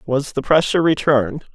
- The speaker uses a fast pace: No, average, 155 wpm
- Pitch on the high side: No, medium, 140 Hz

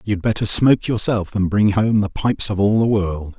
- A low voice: Yes, low, 105 Hz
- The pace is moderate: No, fast, 230 wpm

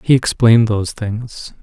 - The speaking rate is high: No, average, 150 wpm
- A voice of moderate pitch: No, low, 115 Hz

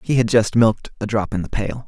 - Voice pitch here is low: Yes, low, 110 Hz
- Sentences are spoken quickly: Yes, fast, 290 wpm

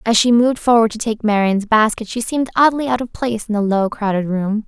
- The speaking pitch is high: Yes, high, 225 Hz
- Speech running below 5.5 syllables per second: No, 6.0 syllables/s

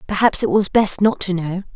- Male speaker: No, female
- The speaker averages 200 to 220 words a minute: No, fast, 240 wpm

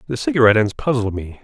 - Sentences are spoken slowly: No, fast, 210 wpm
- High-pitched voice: No, low, 120 Hz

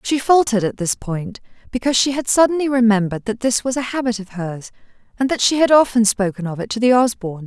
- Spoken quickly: Yes, fast, 225 wpm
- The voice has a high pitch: Yes, high, 230 Hz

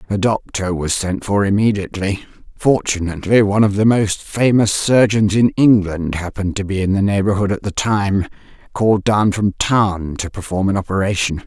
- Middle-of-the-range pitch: No, low, 100 Hz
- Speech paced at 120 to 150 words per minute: No, average, 160 wpm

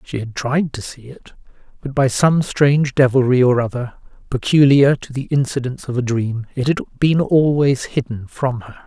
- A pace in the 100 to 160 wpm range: No, average, 185 wpm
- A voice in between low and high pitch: No, low, 130 Hz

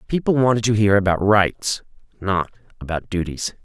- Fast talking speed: No, average, 150 wpm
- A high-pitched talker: No, low, 105 Hz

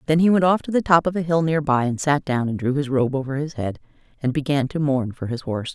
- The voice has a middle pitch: Yes, medium, 145 Hz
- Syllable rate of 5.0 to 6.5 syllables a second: Yes, 6.2 syllables/s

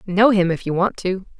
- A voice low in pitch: No, high, 190 Hz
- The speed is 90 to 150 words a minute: No, fast, 260 wpm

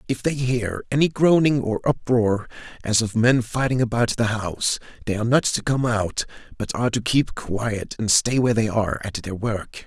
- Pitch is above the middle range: No, low, 115 Hz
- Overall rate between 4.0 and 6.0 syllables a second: Yes, 5.0 syllables/s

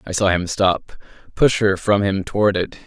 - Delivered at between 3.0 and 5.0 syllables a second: Yes, 4.7 syllables/s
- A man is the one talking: Yes, male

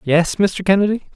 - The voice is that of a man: Yes, male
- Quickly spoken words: No, average, 155 wpm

